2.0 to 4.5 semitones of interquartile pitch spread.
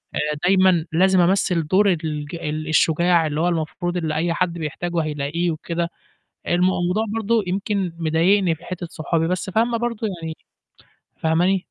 Yes: average, 2.8 semitones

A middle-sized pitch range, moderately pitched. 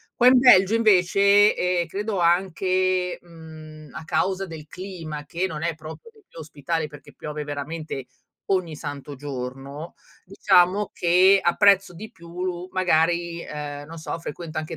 Yes: average, 3.3 semitones; medium, 170 Hz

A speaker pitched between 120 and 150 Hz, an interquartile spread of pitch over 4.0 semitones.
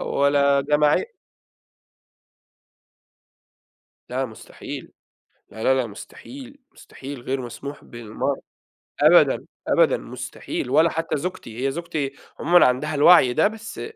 Yes: medium, 140 Hz; average, 4.5 semitones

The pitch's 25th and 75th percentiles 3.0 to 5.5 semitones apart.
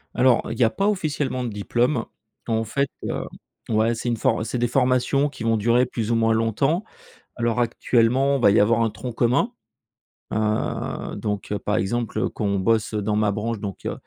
No: narrow, 2.5 semitones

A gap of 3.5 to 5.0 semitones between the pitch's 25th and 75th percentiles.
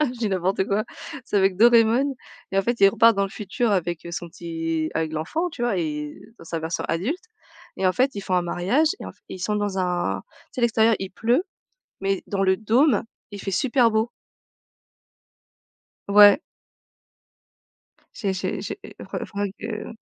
Yes: average, 4.3 semitones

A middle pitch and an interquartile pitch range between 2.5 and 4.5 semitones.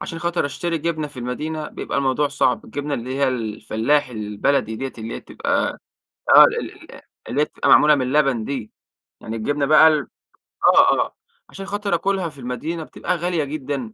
Yes: medium, 145 Hz; average, 4.1 semitones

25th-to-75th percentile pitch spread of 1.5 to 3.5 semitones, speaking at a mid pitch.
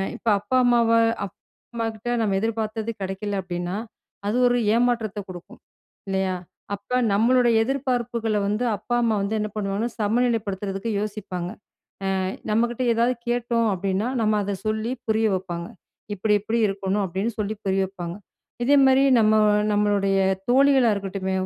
No: average, 3.2 semitones; high, 215 Hz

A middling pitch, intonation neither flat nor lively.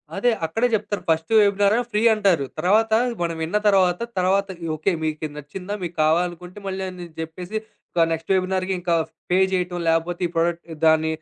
Yes: medium, 180 Hz; average, 3.1 semitones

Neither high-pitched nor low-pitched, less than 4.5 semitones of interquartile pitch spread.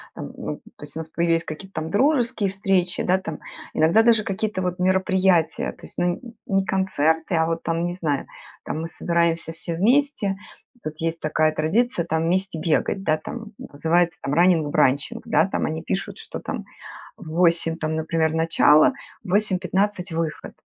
Yes: medium, 170 Hz; average, 3.1 semitones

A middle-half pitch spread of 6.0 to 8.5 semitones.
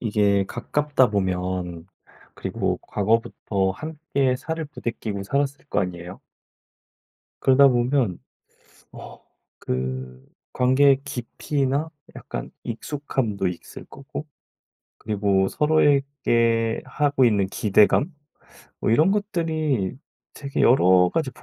Yes: wide, 6.5 semitones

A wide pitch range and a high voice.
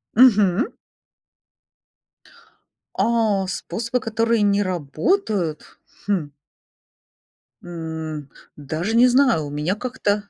Yes: wide, 6.0 semitones; high, 200 Hz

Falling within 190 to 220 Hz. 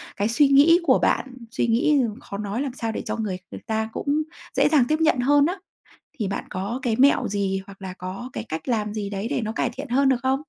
No: high, 235 Hz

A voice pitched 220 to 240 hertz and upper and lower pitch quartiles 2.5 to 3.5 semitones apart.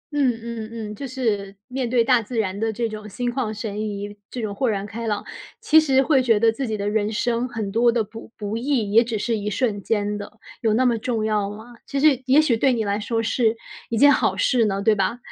Yes: high, 225 Hz; average, 2.8 semitones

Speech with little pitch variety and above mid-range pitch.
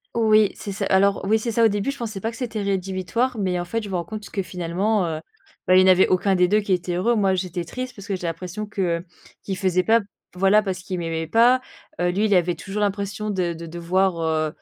No: average, 3.0 semitones; high, 195 Hz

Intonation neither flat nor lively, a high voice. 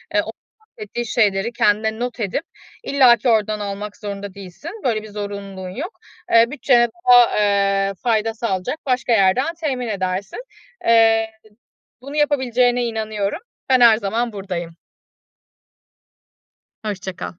Yes: average, 3.5 semitones; high, 220 Hz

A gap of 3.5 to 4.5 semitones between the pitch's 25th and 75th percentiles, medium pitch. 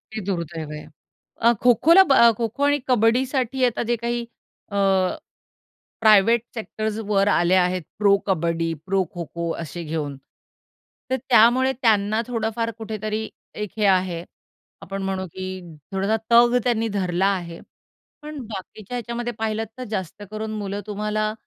No: average, 3.8 semitones; high, 215 Hz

